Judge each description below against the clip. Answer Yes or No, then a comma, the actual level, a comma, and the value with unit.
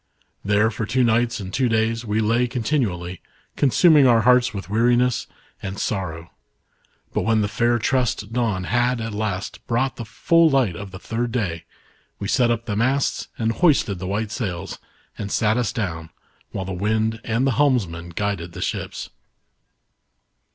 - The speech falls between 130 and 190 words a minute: Yes, average, 165 wpm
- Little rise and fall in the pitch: No, average, 3.4 semitones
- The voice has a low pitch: Yes, low, 110 Hz